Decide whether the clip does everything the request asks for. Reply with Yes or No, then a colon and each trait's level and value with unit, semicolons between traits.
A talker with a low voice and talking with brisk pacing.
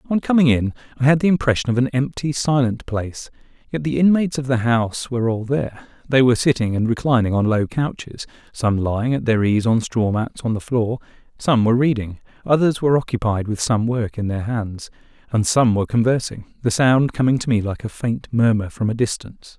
Yes: low, 120 Hz; fast, 210 wpm